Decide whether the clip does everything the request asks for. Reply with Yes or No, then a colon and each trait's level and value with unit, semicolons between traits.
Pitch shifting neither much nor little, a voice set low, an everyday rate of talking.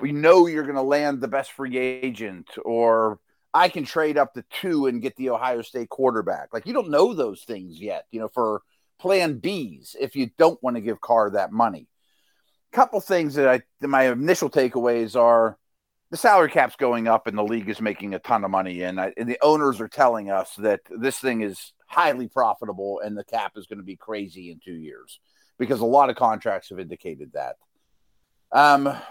No: average, 4.4 semitones; low, 120 Hz; fast, 210 wpm